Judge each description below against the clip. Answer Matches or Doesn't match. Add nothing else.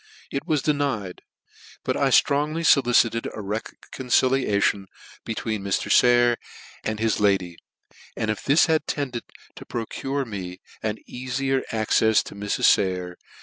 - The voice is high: Doesn't match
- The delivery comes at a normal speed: Doesn't match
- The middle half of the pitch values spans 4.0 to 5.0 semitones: Matches